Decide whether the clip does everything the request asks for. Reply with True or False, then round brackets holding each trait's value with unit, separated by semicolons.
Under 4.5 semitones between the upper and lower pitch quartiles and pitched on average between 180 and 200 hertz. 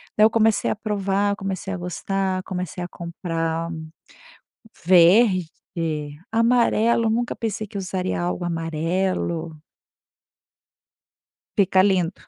True (3.4 semitones; 185 Hz)